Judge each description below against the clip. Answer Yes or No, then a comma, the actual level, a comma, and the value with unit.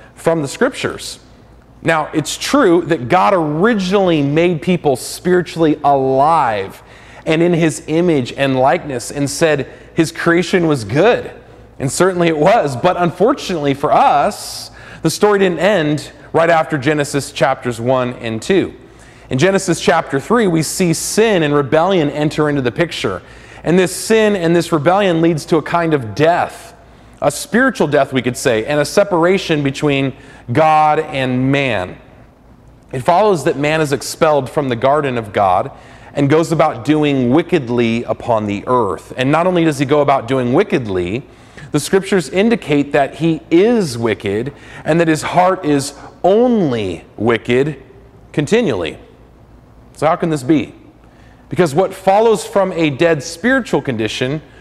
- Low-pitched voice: No, medium, 155 Hz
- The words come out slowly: No, average, 150 wpm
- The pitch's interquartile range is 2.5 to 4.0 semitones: No, average, 4.4 semitones